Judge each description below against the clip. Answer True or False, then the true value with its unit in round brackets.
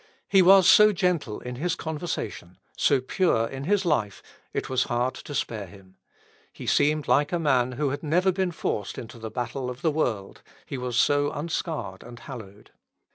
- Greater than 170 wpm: True (185 wpm)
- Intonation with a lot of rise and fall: True (5.7 semitones)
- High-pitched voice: False (135 Hz)